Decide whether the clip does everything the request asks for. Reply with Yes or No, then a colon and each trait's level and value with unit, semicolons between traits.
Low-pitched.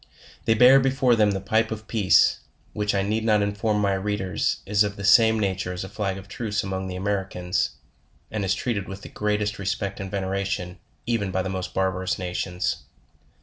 Yes: low, 100 Hz